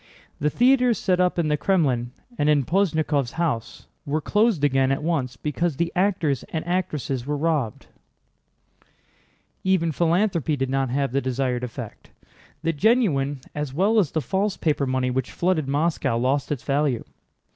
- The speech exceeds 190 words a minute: No, average, 155 wpm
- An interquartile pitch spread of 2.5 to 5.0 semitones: Yes, average, 4.5 semitones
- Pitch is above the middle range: No, medium, 150 Hz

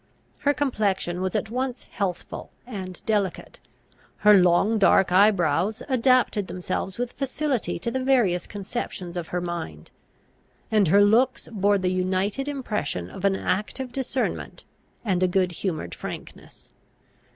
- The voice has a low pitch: No, high, 200 Hz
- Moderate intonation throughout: Yes, average, 4.7 semitones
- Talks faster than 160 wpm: No, average, 140 wpm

